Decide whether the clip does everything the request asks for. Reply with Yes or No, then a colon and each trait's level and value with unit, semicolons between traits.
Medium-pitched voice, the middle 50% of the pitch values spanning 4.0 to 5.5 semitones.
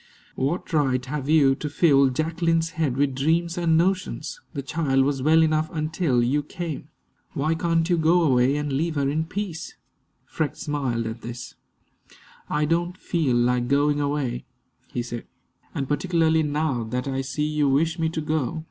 No: medium, 150 Hz; average, 3.3 semitones